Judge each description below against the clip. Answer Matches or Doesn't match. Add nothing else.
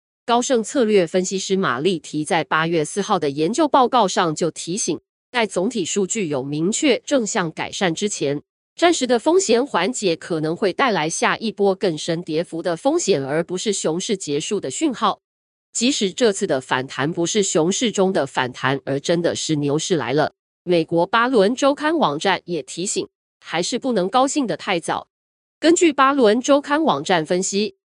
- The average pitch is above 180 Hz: Matches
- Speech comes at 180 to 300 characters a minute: Matches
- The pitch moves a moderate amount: Doesn't match